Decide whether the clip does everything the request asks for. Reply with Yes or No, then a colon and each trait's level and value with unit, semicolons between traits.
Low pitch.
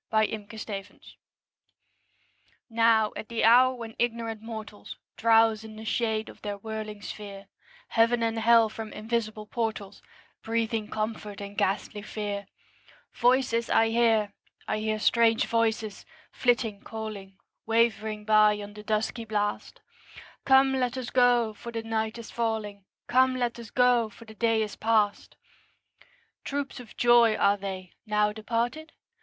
No: high, 220 Hz